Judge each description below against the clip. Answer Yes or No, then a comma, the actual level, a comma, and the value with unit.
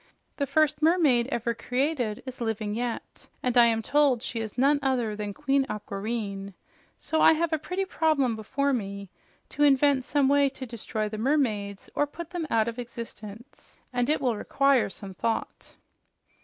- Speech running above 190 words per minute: No, average, 170 wpm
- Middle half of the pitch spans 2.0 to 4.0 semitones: No, average, 4.5 semitones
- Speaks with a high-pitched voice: Yes, high, 245 Hz